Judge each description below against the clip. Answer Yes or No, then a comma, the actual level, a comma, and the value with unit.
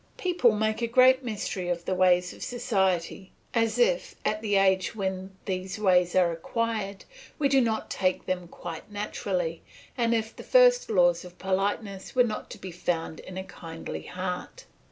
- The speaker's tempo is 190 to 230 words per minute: No, average, 180 wpm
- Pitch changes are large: No, average, 4.0 semitones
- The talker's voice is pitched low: No, high, 195 Hz